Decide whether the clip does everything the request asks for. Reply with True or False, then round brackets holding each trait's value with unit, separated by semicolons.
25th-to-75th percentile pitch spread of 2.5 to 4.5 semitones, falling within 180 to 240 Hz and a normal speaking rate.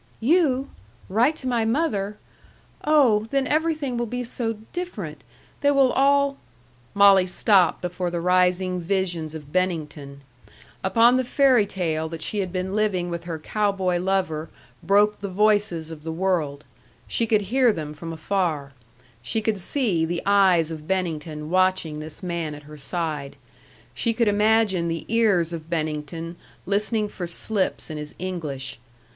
False (5.2 semitones; 185 Hz; 155 wpm)